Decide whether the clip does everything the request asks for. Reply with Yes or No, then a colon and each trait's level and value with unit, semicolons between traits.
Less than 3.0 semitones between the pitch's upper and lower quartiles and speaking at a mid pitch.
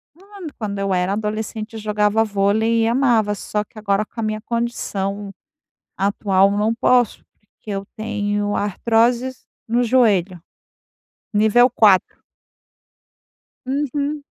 No: narrow, 2.6 semitones; high, 215 Hz